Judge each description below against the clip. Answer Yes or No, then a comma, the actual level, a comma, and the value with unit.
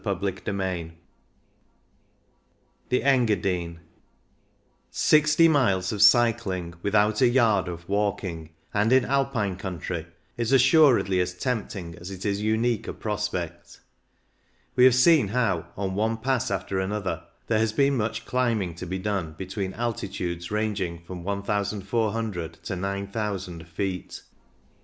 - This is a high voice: No, low, 100 Hz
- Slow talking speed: Yes, slow, 130 wpm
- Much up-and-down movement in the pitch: No, average, 3.9 semitones